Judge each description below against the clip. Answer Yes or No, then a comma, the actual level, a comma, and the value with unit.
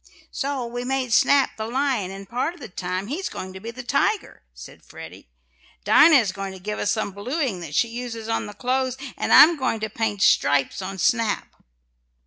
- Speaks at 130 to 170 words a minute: No, average, 200 wpm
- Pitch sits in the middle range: No, high, 230 Hz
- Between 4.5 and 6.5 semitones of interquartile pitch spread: Yes, average, 5.0 semitones